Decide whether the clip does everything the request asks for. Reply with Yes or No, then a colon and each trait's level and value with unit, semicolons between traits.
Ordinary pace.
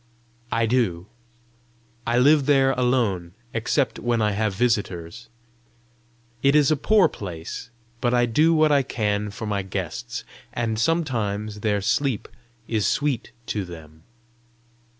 No: slow, 130 wpm